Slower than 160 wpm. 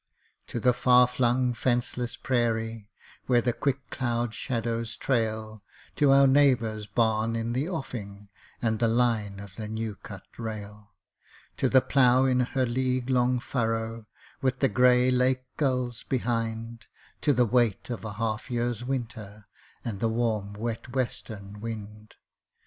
Yes: average, 150 wpm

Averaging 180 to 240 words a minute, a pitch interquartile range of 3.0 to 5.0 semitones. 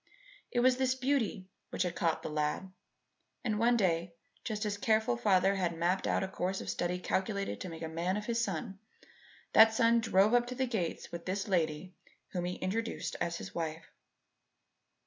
Yes: average, 190 wpm; average, 4.5 semitones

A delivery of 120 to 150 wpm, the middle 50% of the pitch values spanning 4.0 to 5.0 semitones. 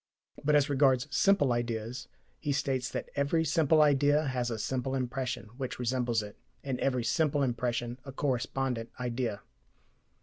No: average, 145 wpm; average, 2.8 semitones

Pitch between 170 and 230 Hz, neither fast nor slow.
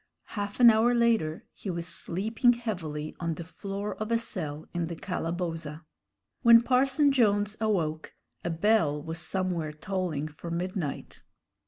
Yes: medium, 185 Hz; average, 145 wpm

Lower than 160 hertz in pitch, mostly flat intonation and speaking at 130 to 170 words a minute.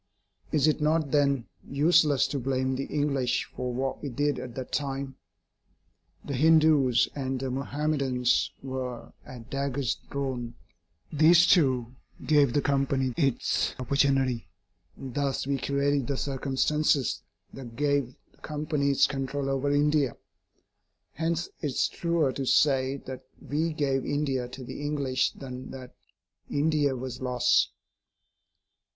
Yes: low, 135 Hz; narrow, 2.0 semitones; slow, 135 wpm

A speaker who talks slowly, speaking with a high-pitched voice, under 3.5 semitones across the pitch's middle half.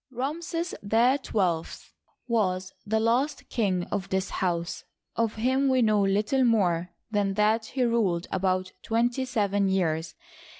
No: slow, 130 wpm; high, 210 Hz; average, 4.3 semitones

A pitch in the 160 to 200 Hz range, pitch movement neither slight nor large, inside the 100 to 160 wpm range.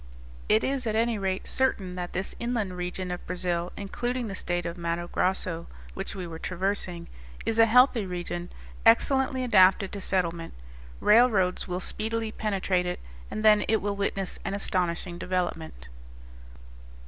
Yes: high, 190 Hz; average, 3.5 semitones; average, 150 wpm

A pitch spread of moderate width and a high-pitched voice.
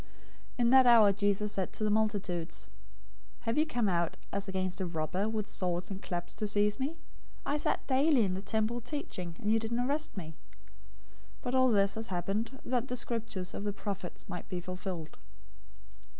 Yes: average, 4.2 semitones; high, 205 Hz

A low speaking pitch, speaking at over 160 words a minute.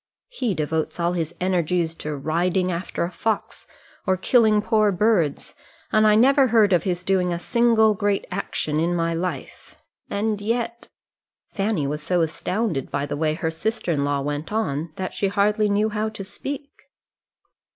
No: medium, 185 Hz; average, 170 wpm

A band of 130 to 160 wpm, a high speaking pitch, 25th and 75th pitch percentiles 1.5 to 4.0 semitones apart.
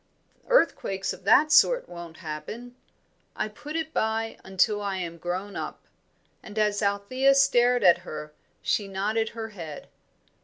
No: average, 145 wpm; high, 205 Hz; average, 4.6 semitones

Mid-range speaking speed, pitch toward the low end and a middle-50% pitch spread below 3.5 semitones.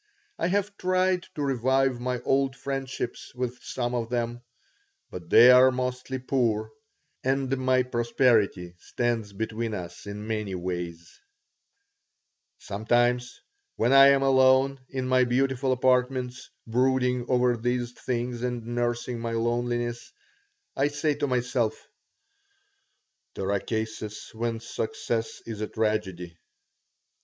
No: slow, 120 wpm; low, 120 Hz; narrow, 2.5 semitones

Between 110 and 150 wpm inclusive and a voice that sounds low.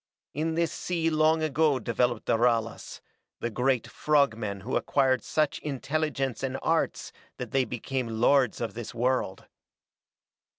Yes: average, 140 wpm; low, 130 Hz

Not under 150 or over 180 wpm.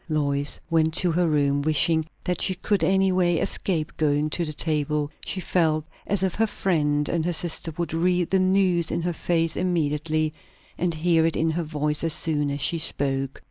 No: average, 195 wpm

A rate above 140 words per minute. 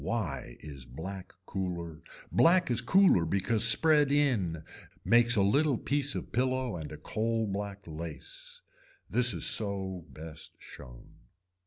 No: slow, 135 wpm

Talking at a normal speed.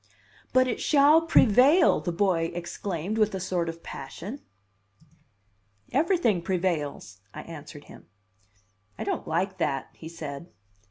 No: slow, 125 wpm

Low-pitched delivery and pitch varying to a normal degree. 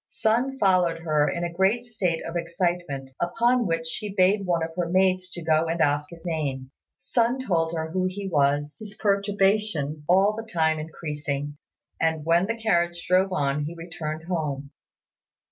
No: medium, 170 Hz; average, 3.6 semitones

